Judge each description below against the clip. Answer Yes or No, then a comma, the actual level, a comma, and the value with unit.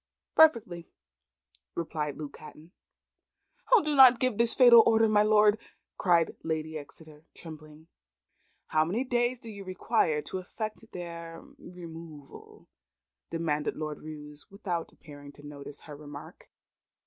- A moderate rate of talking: No, slow, 125 wpm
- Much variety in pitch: Yes, wide, 6.0 semitones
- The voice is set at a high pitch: No, medium, 170 Hz